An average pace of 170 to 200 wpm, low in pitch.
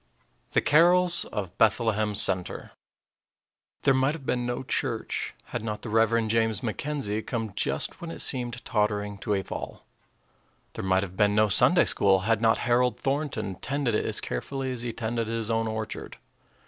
Yes: average, 175 wpm; low, 115 Hz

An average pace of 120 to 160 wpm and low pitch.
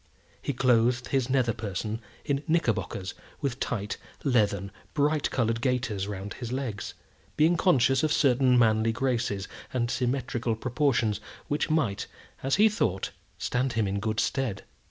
Yes: average, 140 wpm; low, 120 Hz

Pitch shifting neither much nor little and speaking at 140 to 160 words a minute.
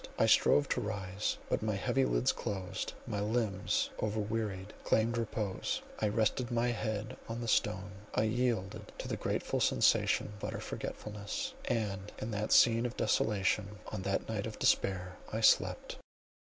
No: narrow, 2.3 semitones; average, 155 wpm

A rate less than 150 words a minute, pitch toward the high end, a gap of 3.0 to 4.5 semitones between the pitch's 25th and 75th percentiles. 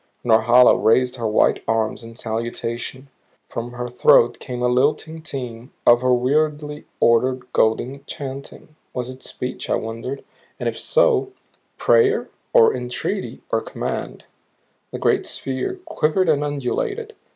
No: slow, 135 wpm; low, 130 Hz; average, 3.9 semitones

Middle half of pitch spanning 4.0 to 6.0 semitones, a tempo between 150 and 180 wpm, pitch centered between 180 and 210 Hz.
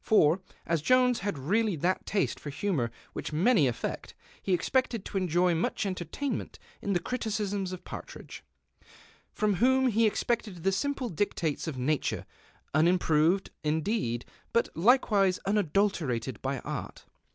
No: wide, 5.4 semitones; average, 140 wpm; high, 190 Hz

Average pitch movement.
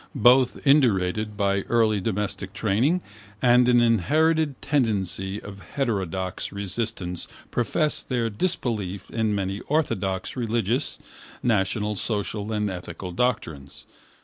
Yes: average, 4.1 semitones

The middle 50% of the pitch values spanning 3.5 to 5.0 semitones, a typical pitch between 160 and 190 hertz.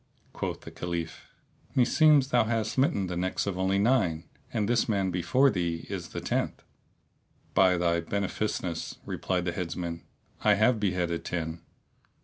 No: average, 4.2 semitones; very low, 95 Hz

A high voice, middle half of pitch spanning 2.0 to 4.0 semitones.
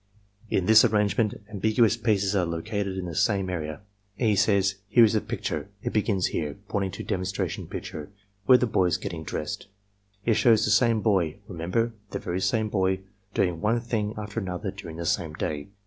No: low, 100 Hz; average, 3.3 semitones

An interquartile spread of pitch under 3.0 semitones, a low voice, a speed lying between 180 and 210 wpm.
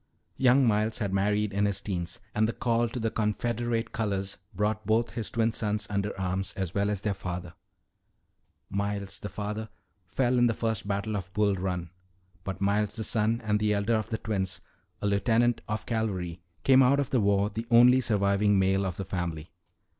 Yes: narrow, 2.5 semitones; low, 105 Hz; average, 185 wpm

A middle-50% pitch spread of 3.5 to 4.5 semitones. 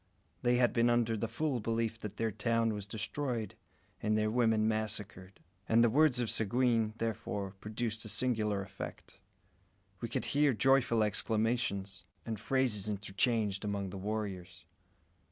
No: narrow, 2.4 semitones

